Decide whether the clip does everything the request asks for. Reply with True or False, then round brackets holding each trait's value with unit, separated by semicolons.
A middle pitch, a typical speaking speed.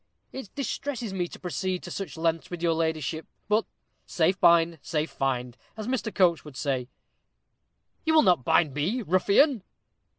True (175 Hz; 160 wpm)